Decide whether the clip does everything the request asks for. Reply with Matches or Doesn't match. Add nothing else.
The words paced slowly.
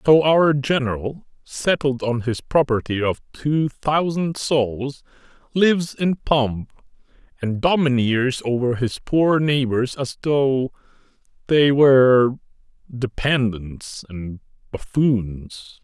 Matches